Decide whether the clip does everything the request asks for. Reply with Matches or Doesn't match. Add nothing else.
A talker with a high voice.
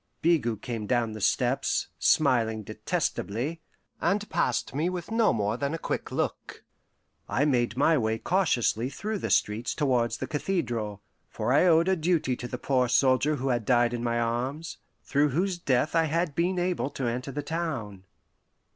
Doesn't match